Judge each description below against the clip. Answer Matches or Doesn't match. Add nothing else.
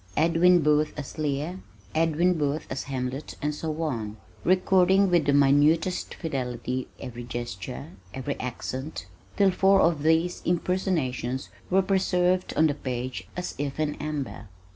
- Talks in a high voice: Doesn't match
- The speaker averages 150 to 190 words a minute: Doesn't match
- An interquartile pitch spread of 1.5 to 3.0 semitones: Doesn't match